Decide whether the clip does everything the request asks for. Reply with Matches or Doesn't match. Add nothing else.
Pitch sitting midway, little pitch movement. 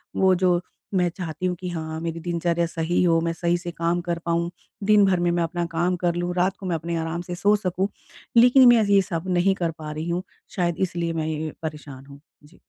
Matches